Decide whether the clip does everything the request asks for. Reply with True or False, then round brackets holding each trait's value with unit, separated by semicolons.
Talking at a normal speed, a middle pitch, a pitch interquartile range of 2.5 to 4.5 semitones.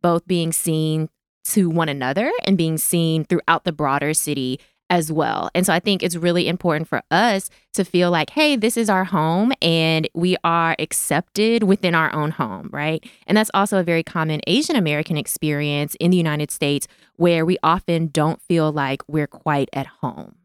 True (190 wpm; 165 Hz; 2.9 semitones)